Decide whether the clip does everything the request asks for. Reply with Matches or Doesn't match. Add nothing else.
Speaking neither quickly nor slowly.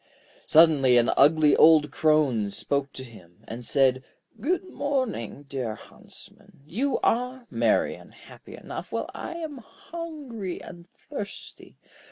Doesn't match